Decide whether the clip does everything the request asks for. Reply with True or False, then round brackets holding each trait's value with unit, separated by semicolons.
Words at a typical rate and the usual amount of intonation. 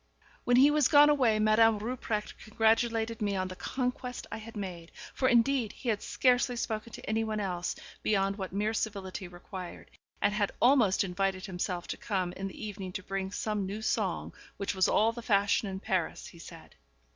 True (185 wpm; 3.1 semitones)